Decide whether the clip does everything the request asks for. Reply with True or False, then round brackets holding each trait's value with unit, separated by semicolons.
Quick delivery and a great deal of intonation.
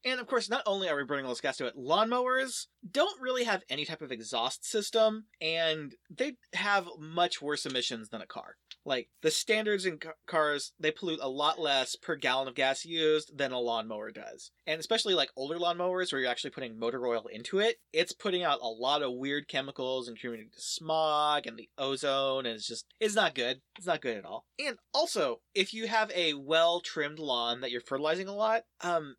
True (215 wpm; 7.4 semitones)